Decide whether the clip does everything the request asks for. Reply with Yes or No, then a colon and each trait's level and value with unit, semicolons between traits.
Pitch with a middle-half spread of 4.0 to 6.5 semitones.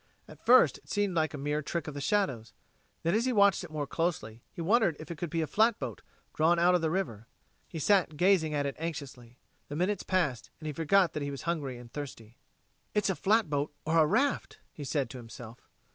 Yes: average, 4.7 semitones